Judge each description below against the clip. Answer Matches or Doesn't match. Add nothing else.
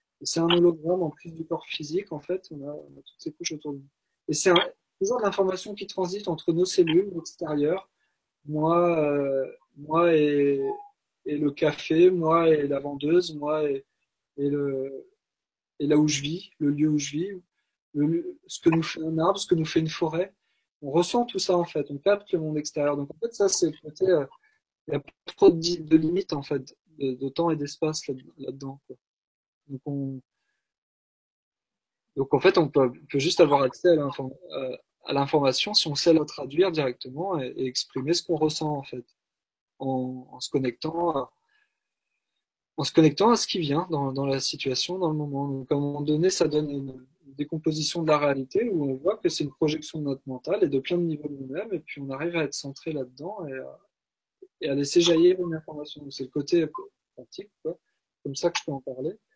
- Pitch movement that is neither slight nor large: Matches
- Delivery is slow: Doesn't match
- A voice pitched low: Doesn't match